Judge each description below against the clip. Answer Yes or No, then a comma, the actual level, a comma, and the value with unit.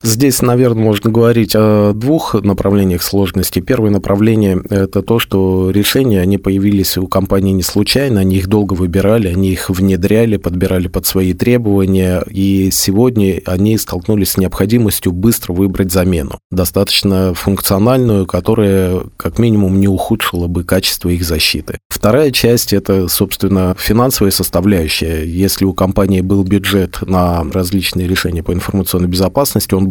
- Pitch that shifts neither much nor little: No, narrow, 2.2 semitones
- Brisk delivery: No, average, 140 wpm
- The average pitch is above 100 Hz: No, very low, 95 Hz